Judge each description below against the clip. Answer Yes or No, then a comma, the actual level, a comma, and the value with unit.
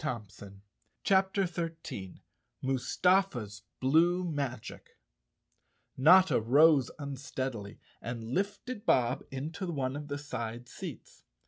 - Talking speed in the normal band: No, slow, 100 wpm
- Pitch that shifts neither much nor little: No, wide, 6.1 semitones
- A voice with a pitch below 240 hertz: Yes, medium, 140 Hz